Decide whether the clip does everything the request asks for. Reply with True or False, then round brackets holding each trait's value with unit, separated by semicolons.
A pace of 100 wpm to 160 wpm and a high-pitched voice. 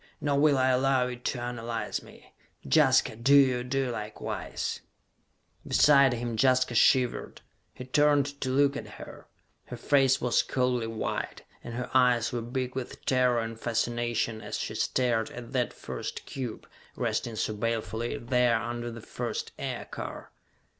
False (150 wpm; 125 Hz)